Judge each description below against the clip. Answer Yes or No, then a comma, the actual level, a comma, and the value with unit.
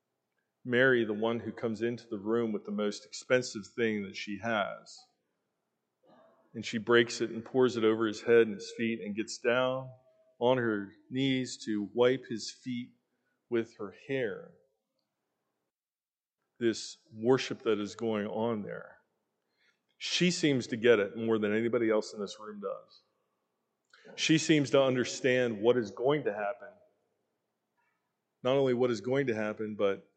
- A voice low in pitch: Yes, low, 115 Hz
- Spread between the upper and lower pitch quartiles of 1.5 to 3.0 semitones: Yes, narrow, 2.6 semitones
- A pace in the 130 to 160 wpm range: Yes, average, 155 wpm